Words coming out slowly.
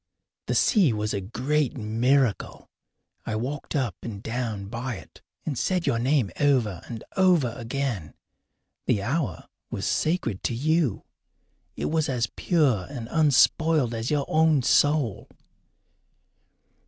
Yes: slow, 130 wpm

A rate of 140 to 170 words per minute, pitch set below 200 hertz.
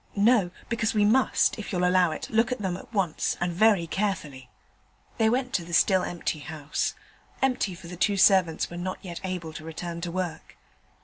No: average, 195 wpm; medium, 185 Hz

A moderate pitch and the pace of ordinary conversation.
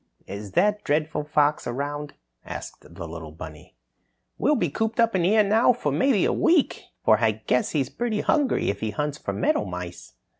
Yes: medium, 150 Hz; average, 175 wpm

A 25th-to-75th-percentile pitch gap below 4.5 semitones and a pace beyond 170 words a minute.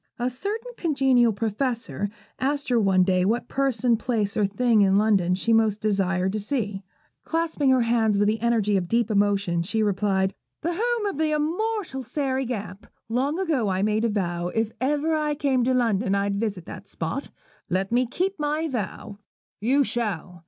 No: wide, 5.4 semitones; average, 180 wpm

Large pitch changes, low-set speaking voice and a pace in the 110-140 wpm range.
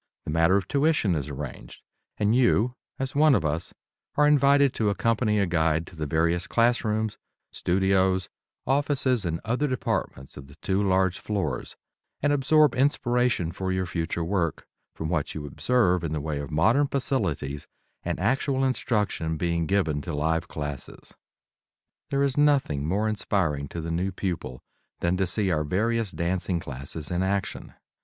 No: wide, 6.8 semitones; very low, 95 Hz; average, 160 wpm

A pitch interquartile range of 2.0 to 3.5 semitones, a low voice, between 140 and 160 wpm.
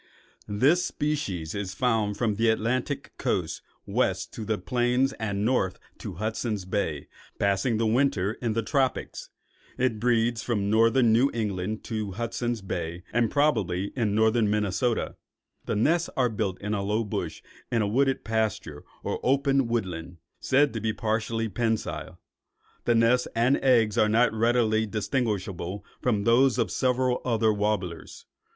Yes: average, 3.1 semitones; low, 110 Hz; average, 150 wpm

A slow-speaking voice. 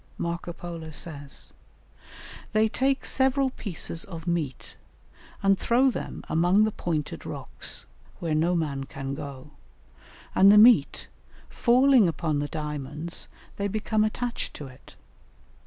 Yes: slow, 125 wpm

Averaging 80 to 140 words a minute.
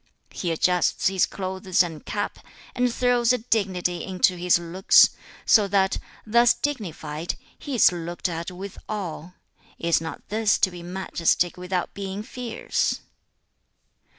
Yes: slow, 135 wpm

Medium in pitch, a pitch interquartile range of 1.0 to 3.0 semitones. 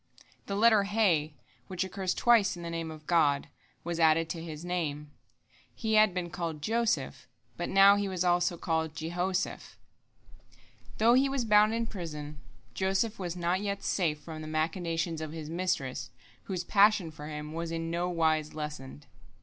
No: medium, 170 Hz; average, 3.8 semitones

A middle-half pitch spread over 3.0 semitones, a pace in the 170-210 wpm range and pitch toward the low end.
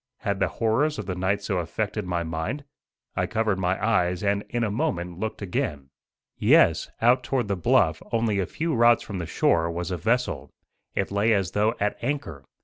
Yes: average, 4.4 semitones; average, 195 wpm; low, 100 Hz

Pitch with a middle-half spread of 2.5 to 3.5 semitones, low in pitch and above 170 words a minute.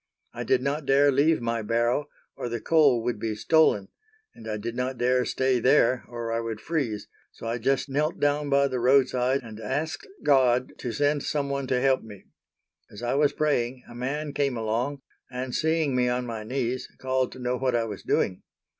Yes: average, 2.9 semitones; low, 125 Hz; average, 200 wpm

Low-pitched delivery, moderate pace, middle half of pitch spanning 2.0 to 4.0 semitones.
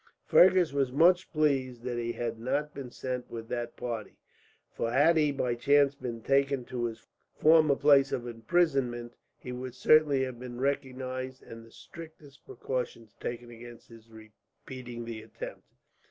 Yes: low, 130 Hz; average, 155 wpm; average, 3.0 semitones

